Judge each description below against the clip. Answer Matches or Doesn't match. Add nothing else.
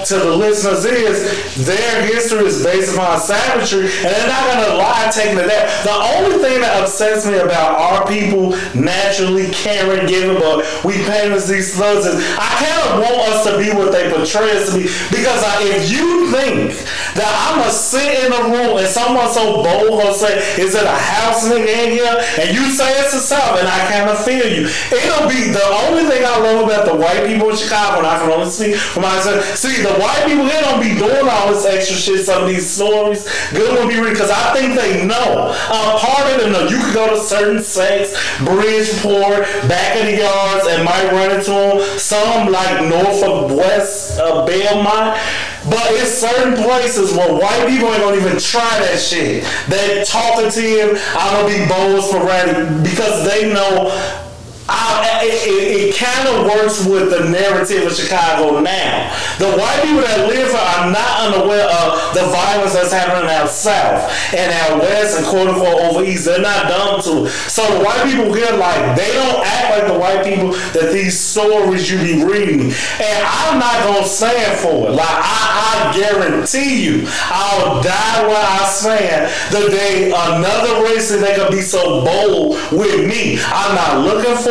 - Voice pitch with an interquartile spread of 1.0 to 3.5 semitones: Matches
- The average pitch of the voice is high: Matches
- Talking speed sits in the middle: Matches